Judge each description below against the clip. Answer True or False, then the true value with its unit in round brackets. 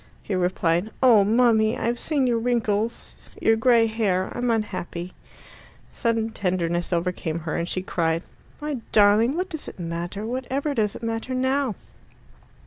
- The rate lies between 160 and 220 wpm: False (145 wpm)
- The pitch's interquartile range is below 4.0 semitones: False (5.0 semitones)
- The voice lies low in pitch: False (220 Hz)